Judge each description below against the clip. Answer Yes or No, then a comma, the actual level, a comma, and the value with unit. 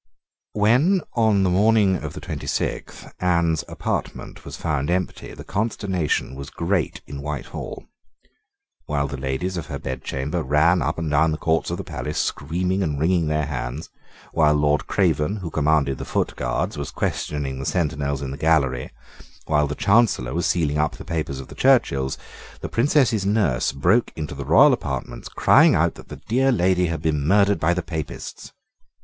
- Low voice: Yes, very low, 80 Hz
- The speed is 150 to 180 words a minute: Yes, average, 175 wpm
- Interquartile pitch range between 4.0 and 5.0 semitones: Yes, average, 4.7 semitones